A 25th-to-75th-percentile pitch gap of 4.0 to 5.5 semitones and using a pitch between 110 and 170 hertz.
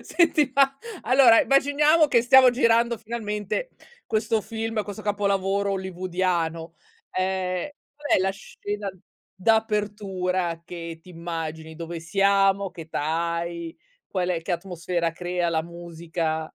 No: average, 4.5 semitones; high, 190 Hz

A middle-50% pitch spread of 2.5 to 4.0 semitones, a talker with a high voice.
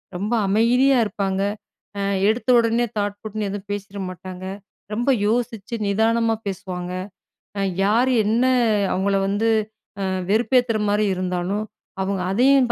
Yes: average, 3.0 semitones; high, 210 Hz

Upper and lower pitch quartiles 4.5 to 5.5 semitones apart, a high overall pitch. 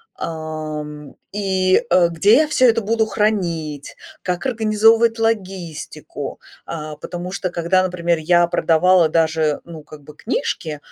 No: average, 4.9 semitones; medium, 175 Hz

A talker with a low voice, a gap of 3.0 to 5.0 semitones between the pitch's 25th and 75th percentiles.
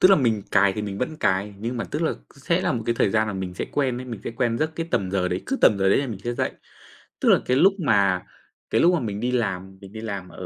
Yes: low, 110 Hz; average, 4.5 semitones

